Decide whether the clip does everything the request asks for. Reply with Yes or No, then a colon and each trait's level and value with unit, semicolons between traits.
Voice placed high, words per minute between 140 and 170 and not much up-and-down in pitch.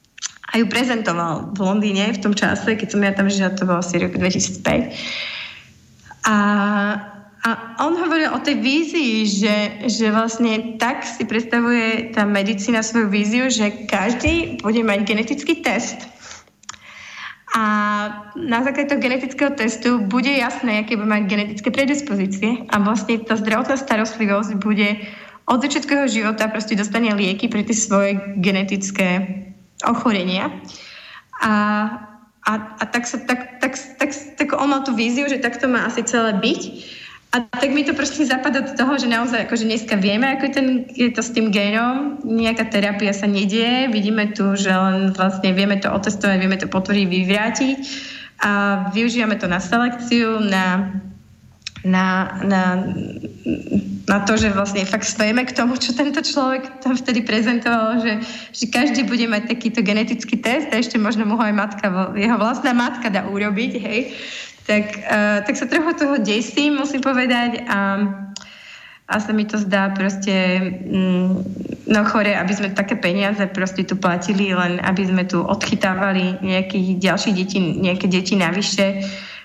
No: high, 215 Hz; average, 155 wpm; average, 3.4 semitones